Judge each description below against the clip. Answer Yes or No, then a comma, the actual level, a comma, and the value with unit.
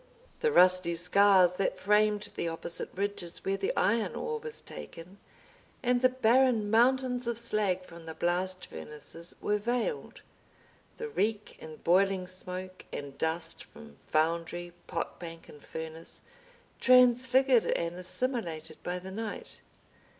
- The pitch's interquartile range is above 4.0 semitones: Yes, wide, 5.6 semitones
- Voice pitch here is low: No, high, 190 Hz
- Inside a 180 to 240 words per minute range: No, slow, 135 wpm